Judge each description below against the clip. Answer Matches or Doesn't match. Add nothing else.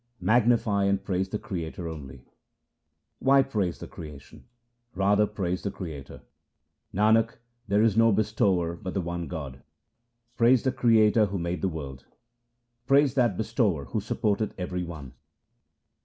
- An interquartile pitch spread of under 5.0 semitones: Matches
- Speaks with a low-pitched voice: Matches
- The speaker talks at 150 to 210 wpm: Doesn't match